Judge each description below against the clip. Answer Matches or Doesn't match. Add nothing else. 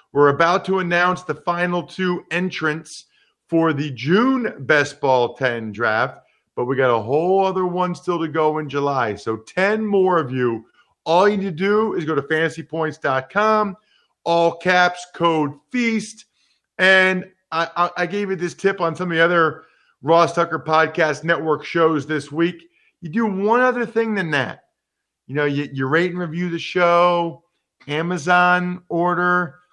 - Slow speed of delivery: Doesn't match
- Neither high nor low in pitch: Matches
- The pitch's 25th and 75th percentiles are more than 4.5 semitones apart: Doesn't match